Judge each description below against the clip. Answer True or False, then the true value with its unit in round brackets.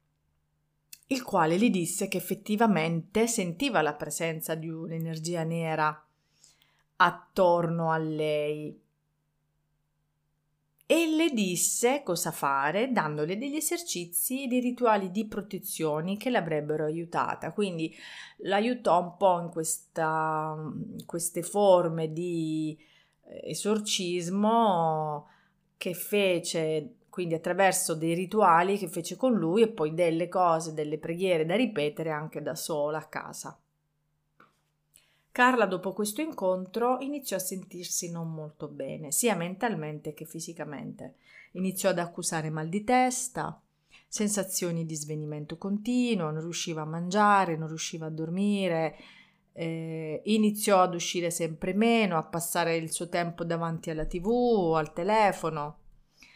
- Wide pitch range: False (4.1 semitones)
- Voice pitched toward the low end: False (170 Hz)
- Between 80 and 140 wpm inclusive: True (120 wpm)